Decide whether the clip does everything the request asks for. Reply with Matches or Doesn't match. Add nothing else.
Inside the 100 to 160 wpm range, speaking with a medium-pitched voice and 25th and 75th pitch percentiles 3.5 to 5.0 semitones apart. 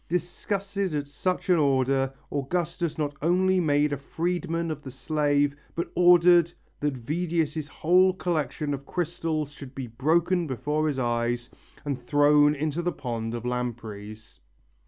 Matches